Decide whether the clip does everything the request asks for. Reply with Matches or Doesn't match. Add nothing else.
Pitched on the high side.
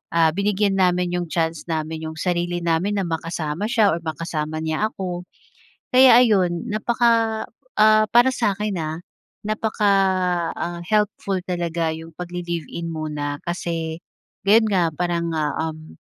Doesn't match